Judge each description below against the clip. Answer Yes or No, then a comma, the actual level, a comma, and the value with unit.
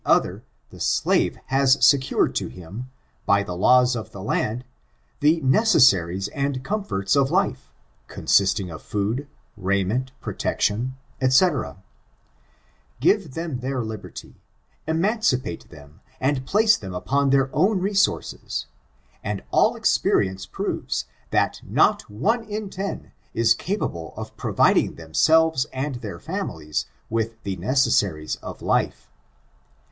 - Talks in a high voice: No, low, 130 Hz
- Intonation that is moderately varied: No, wide, 7.1 semitones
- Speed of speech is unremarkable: No, slow, 125 wpm